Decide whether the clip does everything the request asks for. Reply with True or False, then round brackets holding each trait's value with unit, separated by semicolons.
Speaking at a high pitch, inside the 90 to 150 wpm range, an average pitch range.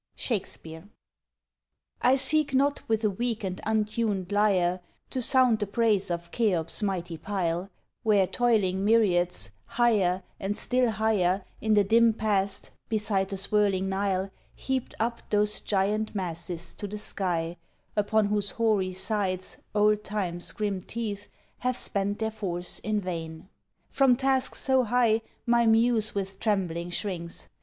True (205 Hz; 140 wpm; 3.1 semitones)